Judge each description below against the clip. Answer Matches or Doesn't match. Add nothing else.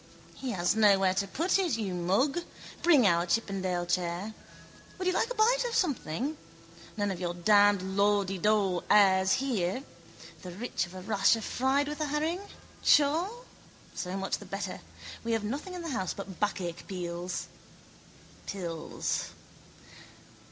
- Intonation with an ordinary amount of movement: Doesn't match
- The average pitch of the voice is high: Matches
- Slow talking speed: Doesn't match